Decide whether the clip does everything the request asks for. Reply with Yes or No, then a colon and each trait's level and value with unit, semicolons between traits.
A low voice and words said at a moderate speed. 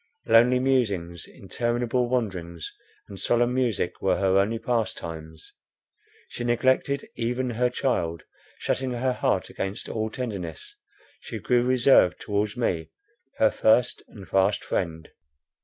No: low, 115 Hz; slow, 125 wpm